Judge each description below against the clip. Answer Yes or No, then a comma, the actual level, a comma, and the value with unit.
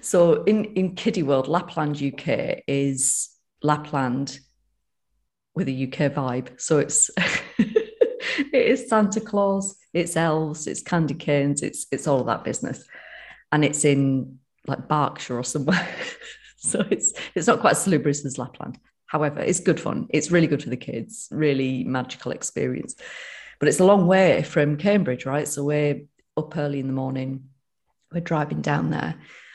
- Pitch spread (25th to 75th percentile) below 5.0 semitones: No, wide, 5.5 semitones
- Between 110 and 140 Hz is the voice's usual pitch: No, medium, 150 Hz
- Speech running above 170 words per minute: No, average, 160 wpm